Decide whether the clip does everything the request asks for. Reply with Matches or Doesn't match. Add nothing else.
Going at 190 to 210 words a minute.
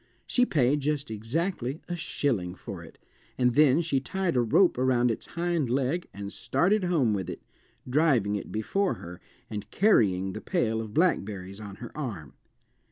Doesn't match